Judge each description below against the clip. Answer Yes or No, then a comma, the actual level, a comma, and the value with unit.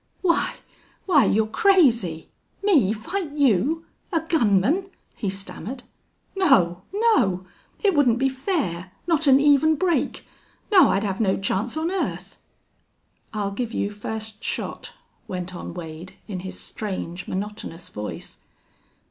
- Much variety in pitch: Yes, wide, 8.9 semitones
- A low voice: No, high, 225 Hz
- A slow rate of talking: Yes, slow, 130 wpm